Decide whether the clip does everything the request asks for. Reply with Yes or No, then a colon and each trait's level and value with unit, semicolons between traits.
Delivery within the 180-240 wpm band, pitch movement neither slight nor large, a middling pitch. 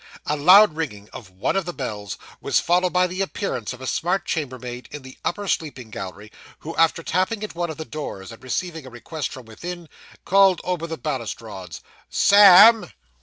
No: average, 185 wpm; wide, 6.7 semitones; medium, 160 Hz